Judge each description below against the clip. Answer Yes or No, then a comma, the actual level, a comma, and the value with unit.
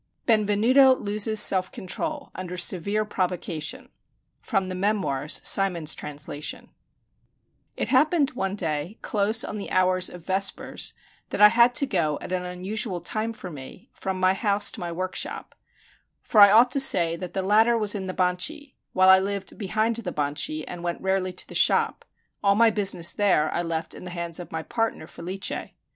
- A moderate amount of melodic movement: Yes, average, 3.3 semitones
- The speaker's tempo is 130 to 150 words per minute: No, average, 175 wpm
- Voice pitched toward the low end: No, high, 190 Hz